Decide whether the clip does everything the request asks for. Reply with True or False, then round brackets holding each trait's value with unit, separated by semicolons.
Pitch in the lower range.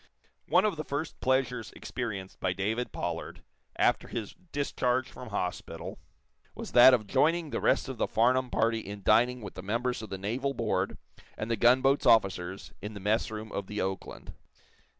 True (115 Hz)